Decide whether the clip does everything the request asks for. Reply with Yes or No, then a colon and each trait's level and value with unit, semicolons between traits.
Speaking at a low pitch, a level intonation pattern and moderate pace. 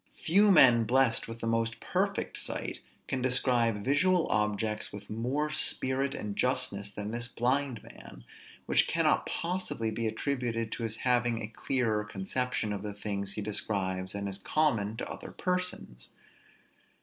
No: low, 115 Hz; average, 3.8 semitones; average, 150 wpm